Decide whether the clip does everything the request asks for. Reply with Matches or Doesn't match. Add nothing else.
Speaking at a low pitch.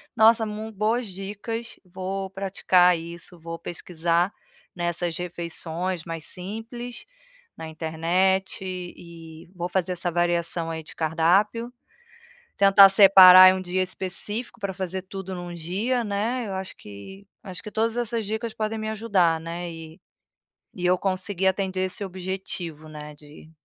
Doesn't match